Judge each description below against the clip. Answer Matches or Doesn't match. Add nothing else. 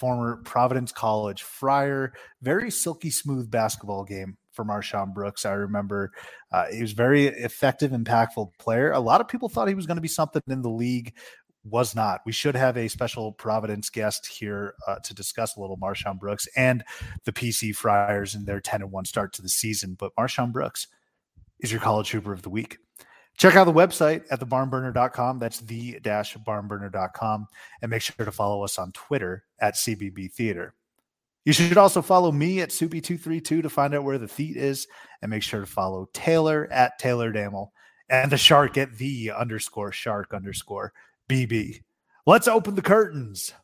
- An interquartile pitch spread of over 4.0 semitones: Matches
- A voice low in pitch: Matches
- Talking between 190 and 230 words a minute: Doesn't match